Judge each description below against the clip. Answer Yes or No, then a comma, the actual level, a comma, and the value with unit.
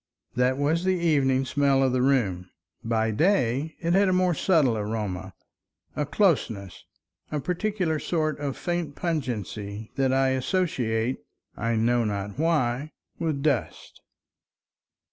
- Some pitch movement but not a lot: No, wide, 6.2 semitones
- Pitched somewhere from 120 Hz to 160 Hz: Yes, low, 135 Hz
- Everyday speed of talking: No, slow, 125 wpm